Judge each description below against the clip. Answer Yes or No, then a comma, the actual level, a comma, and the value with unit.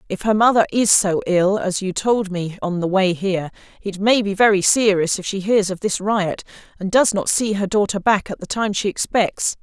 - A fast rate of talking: Yes, fast, 230 wpm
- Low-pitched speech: No, high, 200 Hz